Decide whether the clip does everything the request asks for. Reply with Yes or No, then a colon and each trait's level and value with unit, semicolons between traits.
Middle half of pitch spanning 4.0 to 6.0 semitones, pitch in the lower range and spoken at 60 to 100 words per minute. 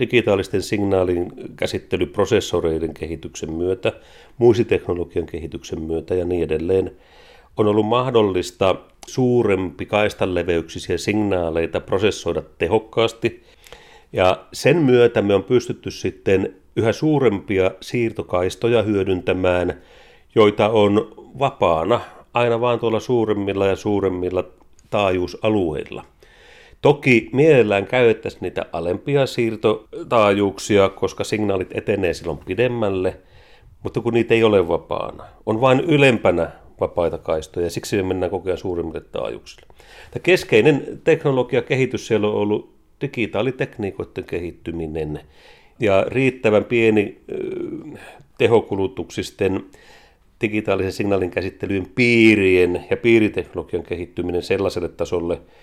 Yes: average, 4.4 semitones; low, 105 Hz; slow, 95 wpm